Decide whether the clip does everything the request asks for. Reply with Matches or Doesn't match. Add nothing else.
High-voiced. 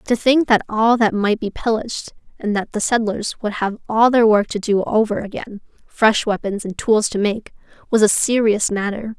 Matches